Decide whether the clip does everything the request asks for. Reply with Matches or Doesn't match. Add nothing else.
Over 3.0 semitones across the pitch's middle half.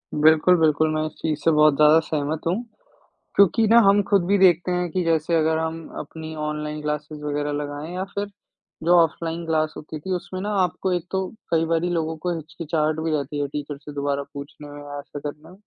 Doesn't match